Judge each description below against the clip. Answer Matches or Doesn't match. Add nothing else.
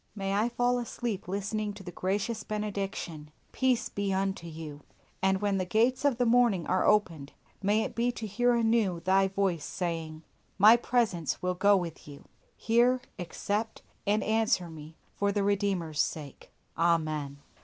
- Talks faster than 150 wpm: Matches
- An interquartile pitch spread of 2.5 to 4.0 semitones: Doesn't match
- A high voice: Matches